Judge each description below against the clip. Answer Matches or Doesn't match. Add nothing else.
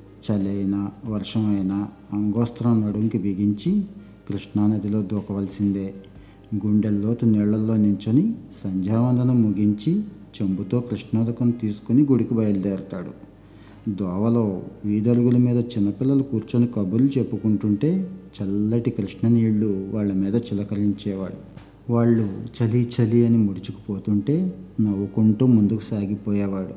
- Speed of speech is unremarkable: Matches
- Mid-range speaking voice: Doesn't match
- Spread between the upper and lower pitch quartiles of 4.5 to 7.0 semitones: Doesn't match